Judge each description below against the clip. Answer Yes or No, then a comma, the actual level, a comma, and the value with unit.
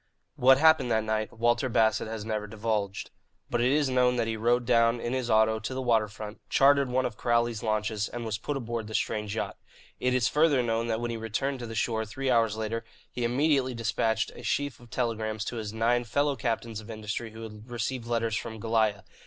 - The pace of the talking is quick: Yes, fast, 220 wpm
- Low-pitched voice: Yes, low, 115 Hz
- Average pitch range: No, narrow, 2.1 semitones